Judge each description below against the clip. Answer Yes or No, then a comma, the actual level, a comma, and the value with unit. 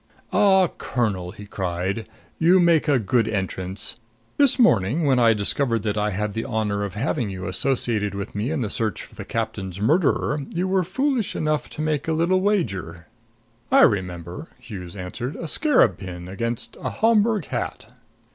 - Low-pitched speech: Yes, low, 115 Hz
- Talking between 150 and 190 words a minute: Yes, average, 175 wpm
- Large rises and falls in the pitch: Yes, wide, 8.2 semitones